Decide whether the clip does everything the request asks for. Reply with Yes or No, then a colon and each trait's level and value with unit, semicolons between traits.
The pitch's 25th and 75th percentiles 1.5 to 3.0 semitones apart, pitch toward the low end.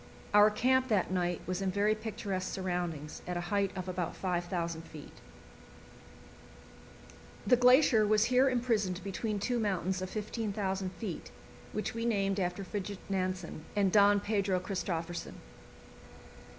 No: average, 2.7 semitones; high, 195 Hz